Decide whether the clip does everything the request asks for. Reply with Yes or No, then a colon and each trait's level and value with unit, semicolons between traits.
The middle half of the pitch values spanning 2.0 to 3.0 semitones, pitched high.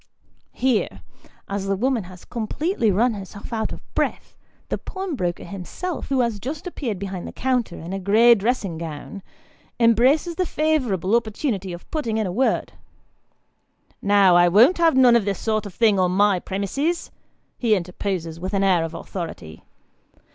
No: average, 5.1 semitones; high, 210 Hz